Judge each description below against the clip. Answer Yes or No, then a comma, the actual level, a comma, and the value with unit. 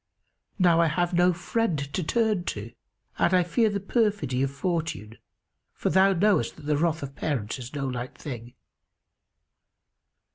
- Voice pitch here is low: No, medium, 165 Hz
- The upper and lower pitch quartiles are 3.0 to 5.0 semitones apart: No, wide, 5.4 semitones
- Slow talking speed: No, average, 155 wpm